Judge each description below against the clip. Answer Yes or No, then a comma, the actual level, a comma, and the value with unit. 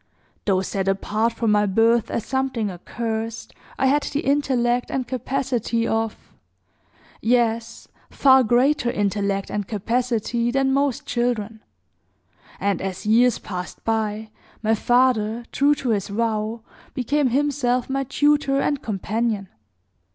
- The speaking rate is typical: No, slow, 125 wpm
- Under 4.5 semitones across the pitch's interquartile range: Yes, average, 3.4 semitones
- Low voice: No, high, 230 Hz